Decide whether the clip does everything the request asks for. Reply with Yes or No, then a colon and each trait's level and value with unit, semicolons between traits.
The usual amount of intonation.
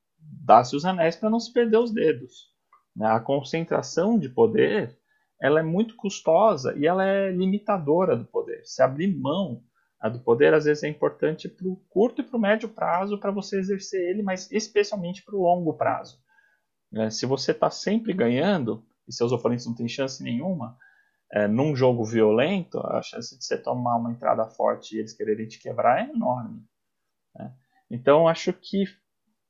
No: wide, 7.6 semitones